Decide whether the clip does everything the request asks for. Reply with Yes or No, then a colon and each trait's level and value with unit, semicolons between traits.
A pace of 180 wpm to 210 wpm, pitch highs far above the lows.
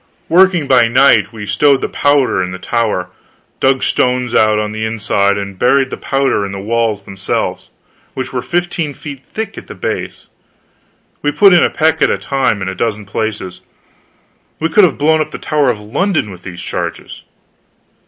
Yes: average, 185 wpm; wide, 6.1 semitones